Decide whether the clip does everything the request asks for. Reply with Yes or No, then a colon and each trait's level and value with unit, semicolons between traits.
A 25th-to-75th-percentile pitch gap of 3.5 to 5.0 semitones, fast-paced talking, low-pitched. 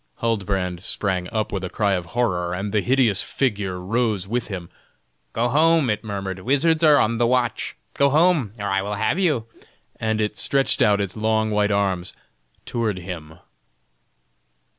No: average, 4.0 semitones; average, 165 wpm; low, 105 Hz